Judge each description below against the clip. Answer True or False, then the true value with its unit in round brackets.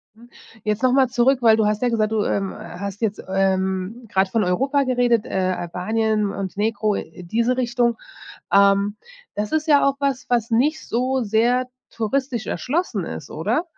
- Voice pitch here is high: True (225 Hz)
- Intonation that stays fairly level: False (4.0 semitones)